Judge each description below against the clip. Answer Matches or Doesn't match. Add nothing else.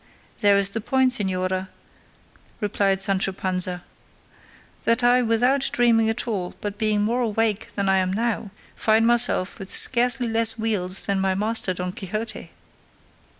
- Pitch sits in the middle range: Doesn't match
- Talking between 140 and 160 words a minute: Matches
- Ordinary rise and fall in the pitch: Matches